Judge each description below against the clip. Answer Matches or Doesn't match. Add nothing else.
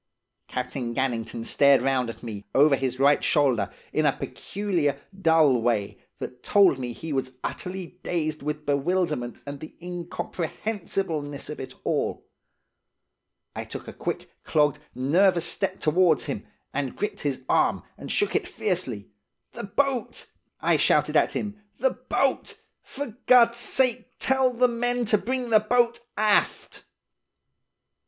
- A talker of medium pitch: Matches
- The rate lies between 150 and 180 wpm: Doesn't match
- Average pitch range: Doesn't match